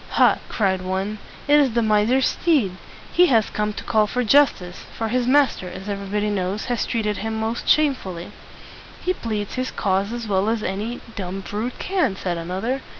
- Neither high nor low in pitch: No, high, 215 Hz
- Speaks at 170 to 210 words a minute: Yes, average, 190 wpm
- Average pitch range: Yes, average, 4.2 semitones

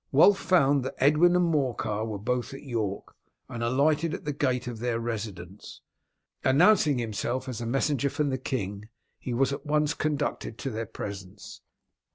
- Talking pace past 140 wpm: Yes, average, 170 wpm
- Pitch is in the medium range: No, low, 130 Hz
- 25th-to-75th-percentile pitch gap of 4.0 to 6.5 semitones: Yes, average, 4.5 semitones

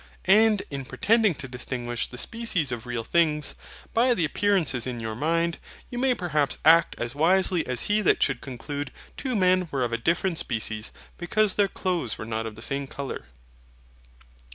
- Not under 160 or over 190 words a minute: Yes, average, 175 wpm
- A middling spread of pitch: No, wide, 7.3 semitones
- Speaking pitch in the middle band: Yes, medium, 150 Hz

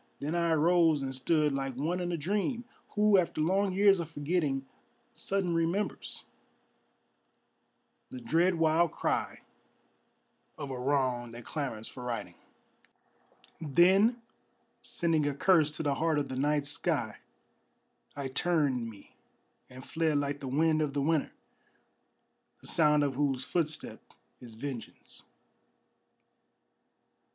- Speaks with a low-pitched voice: No, medium, 150 Hz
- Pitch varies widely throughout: No, average, 3.9 semitones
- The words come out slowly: Yes, slow, 125 wpm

